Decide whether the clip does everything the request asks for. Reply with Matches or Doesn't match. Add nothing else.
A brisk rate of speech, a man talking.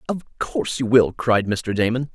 Doesn't match